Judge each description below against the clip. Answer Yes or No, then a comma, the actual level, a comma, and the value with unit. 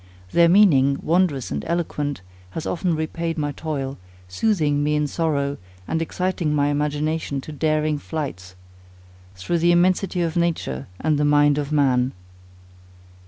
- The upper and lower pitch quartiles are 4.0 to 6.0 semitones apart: No, average, 2.9 semitones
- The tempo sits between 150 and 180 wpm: No, average, 140 wpm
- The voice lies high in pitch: No, medium, 150 Hz